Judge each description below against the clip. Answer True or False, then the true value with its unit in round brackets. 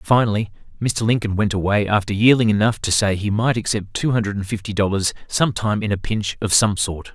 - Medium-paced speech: False (210 wpm)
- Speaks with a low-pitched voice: True (105 Hz)